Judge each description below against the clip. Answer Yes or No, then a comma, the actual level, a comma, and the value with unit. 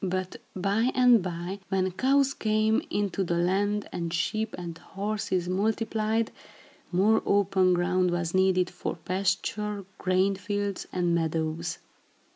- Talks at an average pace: No, slow, 125 wpm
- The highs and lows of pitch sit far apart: No, average, 2.9 semitones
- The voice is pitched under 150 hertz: No, high, 190 Hz